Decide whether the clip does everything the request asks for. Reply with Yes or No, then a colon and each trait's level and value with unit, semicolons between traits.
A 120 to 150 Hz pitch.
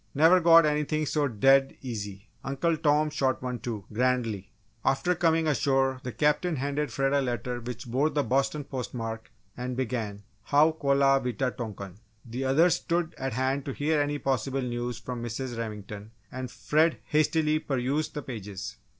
Yes: low, 135 Hz